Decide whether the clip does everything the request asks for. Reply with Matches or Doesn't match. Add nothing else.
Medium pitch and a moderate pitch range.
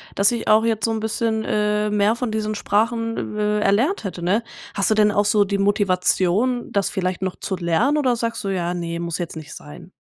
Doesn't match